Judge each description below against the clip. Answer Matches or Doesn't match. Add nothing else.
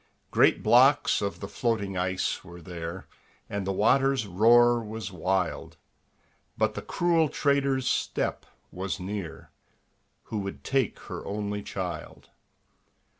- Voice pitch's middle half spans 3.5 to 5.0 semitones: Matches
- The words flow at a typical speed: Doesn't match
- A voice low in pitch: Matches